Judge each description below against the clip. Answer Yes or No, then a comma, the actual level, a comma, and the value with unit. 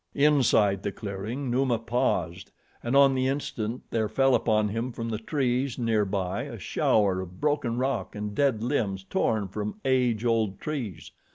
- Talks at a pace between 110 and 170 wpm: Yes, average, 165 wpm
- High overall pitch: No, low, 115 Hz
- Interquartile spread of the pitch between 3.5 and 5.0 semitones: Yes, average, 4.1 semitones